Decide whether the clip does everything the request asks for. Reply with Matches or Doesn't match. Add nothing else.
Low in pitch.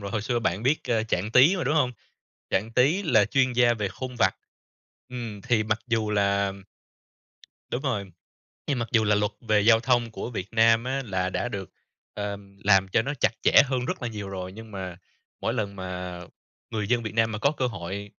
Matches